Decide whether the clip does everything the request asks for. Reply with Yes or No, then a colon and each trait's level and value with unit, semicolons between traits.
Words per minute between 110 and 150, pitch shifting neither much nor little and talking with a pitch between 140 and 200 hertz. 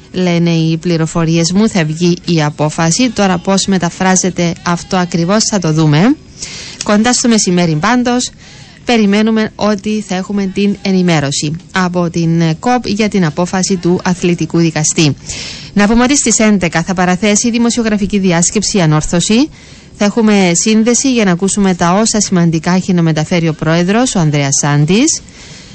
Yes: average, 145 wpm; average, 4.0 semitones; medium, 185 Hz